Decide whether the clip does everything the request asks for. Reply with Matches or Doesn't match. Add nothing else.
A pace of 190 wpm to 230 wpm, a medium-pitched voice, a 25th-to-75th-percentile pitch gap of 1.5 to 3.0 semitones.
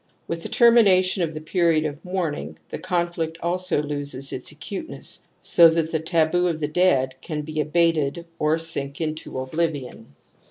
Doesn't match